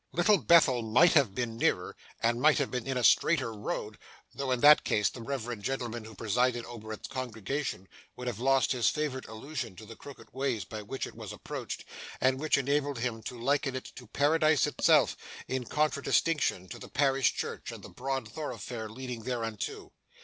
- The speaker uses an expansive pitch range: No, average, 3.6 semitones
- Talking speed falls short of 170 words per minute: No, average, 185 wpm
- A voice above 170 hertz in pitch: No, low, 125 Hz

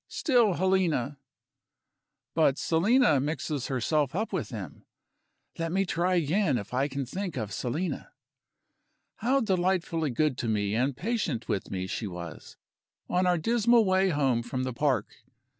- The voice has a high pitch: No, medium, 155 Hz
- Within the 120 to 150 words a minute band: Yes, average, 145 wpm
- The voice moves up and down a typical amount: No, wide, 6.9 semitones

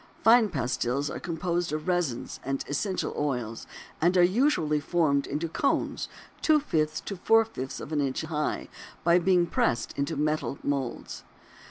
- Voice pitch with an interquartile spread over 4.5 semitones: No, average, 4.2 semitones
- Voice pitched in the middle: Yes, medium, 155 Hz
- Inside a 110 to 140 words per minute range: No, average, 155 wpm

